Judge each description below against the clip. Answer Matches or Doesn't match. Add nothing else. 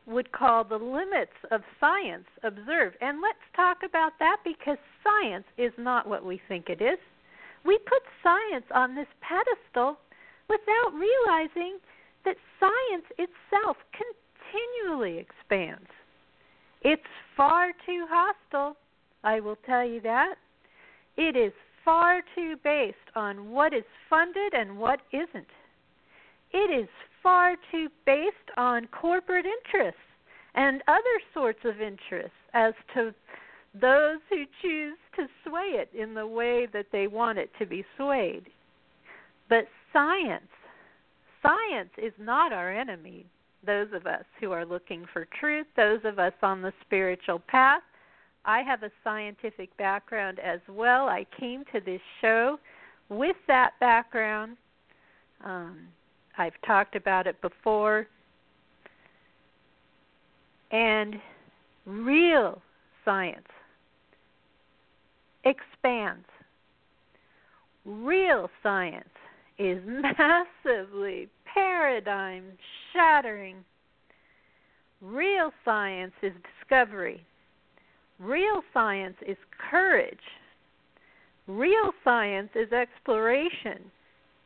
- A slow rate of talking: Matches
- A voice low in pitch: Doesn't match